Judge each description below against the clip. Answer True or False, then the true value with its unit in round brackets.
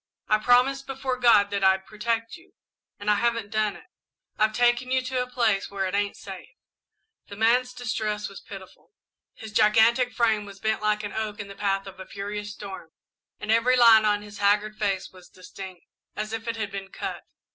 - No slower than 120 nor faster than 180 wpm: False (200 wpm)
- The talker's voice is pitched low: False (215 Hz)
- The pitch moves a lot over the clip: False (2.7 semitones)